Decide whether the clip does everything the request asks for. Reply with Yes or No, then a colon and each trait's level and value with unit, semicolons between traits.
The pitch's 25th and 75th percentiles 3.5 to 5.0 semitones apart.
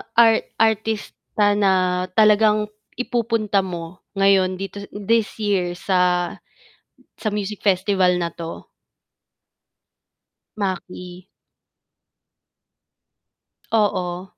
No: average, 2.7 semitones